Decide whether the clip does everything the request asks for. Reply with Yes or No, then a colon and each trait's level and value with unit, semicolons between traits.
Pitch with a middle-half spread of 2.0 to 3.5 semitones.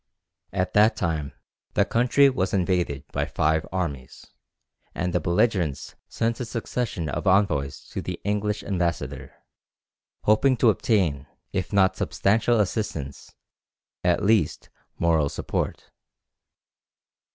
No: average, 5.2 semitones